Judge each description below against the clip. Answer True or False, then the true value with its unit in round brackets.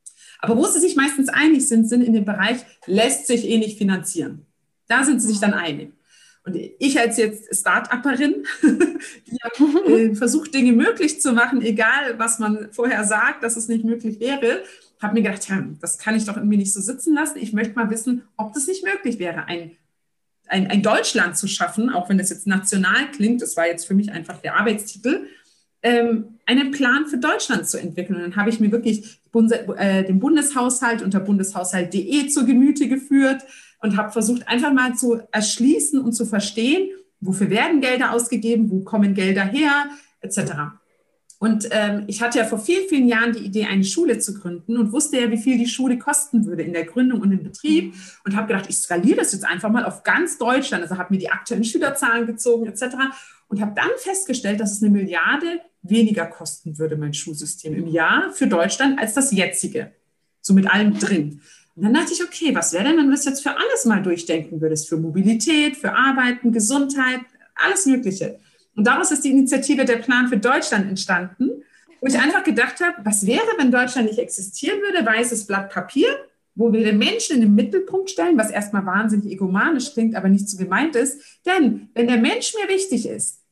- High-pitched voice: True (230 Hz)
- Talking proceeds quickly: True (195 wpm)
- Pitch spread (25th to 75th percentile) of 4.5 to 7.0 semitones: True (5.2 semitones)